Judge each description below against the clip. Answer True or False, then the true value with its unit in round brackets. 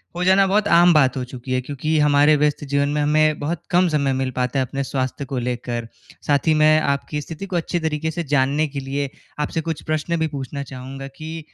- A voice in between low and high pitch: True (145 Hz)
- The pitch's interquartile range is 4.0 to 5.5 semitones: False (2.9 semitones)